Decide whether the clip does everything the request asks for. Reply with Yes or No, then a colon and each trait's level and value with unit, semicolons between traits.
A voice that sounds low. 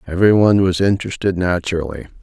Yes: very low, 90 Hz